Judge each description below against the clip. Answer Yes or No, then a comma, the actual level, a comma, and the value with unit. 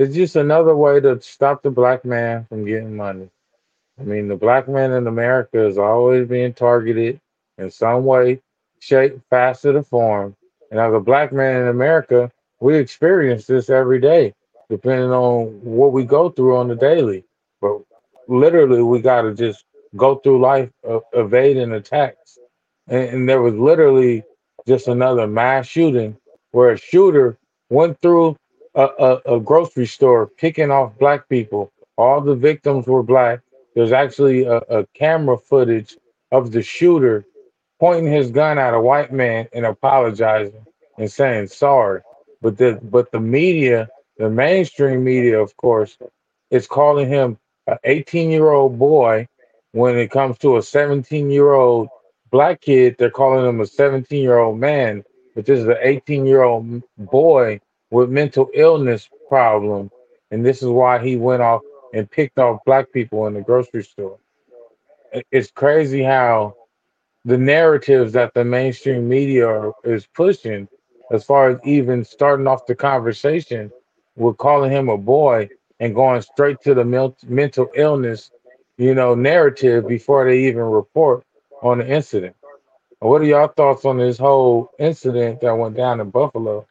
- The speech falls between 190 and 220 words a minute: No, average, 160 wpm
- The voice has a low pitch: Yes, low, 125 Hz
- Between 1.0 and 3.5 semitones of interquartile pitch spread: Yes, average, 2.9 semitones